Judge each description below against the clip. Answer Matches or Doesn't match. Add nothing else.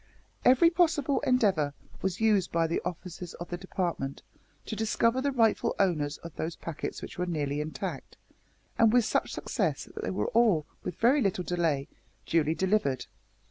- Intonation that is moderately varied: Doesn't match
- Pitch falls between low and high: Matches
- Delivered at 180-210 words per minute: Doesn't match